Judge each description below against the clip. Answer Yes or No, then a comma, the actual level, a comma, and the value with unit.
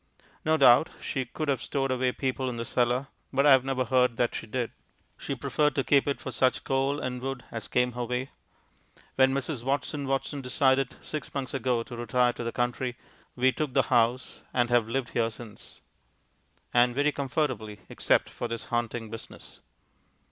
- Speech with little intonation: Yes, narrow, 2.0 semitones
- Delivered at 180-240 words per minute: Yes, average, 185 wpm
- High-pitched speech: No, low, 130 Hz